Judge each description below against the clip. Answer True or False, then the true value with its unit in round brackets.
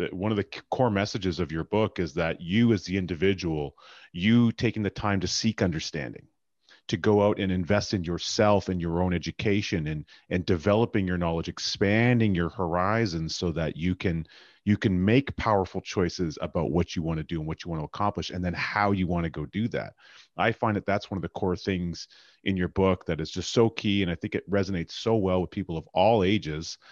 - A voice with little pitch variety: False (3.4 semitones)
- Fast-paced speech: True (220 wpm)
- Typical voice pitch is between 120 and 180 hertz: False (95 Hz)